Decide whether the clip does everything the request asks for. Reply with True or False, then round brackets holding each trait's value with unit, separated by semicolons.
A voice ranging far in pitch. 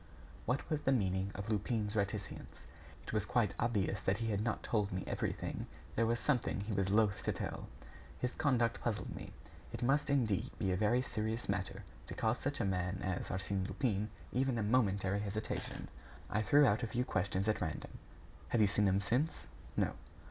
False (3.4 semitones)